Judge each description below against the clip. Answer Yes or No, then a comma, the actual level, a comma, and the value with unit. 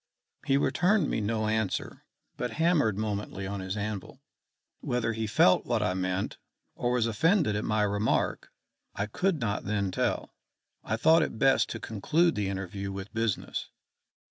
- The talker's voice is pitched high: No, low, 110 Hz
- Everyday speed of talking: Yes, average, 160 wpm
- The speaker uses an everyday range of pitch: Yes, average, 3.6 semitones